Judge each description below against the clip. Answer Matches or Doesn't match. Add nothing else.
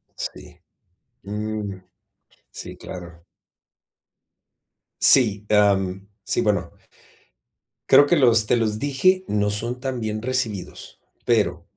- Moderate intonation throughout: Matches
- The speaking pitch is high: Doesn't match